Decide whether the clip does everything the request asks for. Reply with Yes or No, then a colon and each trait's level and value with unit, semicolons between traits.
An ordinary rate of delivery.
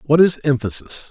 Yes: average, 165 wpm